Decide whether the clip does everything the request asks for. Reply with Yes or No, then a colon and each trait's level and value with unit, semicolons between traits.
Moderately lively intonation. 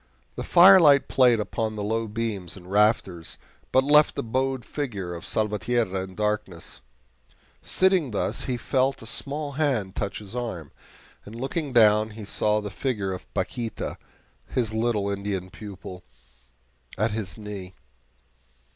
Yes: average, 4.4 semitones